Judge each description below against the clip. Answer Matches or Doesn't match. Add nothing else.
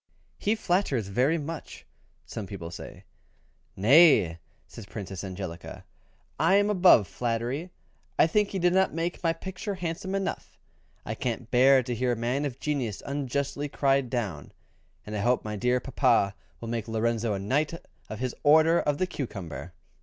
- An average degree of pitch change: Doesn't match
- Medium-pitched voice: Doesn't match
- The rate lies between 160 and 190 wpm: Matches